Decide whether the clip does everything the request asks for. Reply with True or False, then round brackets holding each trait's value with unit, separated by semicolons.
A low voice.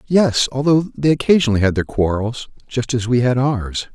True (125 Hz)